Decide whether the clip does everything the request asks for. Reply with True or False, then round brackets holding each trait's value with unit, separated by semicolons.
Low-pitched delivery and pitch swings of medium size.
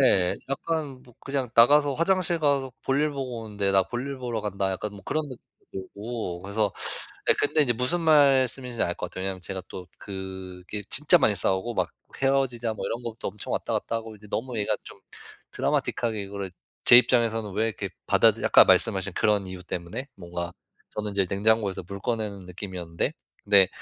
True (110 Hz; 5.0 semitones)